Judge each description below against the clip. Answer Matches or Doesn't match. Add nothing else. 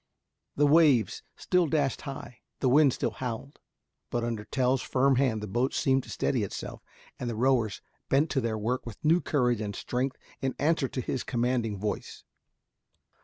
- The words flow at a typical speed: Matches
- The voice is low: Matches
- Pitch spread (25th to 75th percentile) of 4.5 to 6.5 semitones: Doesn't match